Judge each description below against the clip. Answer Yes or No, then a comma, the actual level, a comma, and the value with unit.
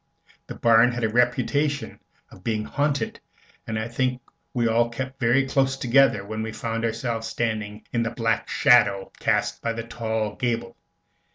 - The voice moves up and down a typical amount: No, narrow, 2.1 semitones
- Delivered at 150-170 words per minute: Yes, average, 165 wpm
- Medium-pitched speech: No, low, 115 Hz